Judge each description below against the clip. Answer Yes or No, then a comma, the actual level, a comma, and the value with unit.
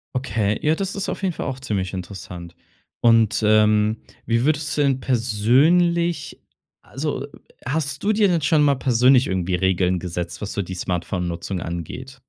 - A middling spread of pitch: No, wide, 7.5 semitones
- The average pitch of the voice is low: Yes, low, 115 Hz